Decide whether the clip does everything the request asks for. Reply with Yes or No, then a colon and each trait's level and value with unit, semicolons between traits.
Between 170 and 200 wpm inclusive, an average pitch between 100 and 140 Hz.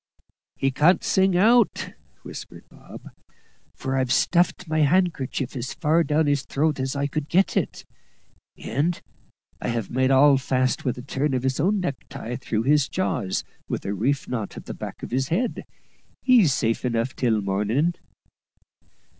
No: average, 160 wpm; low, 135 Hz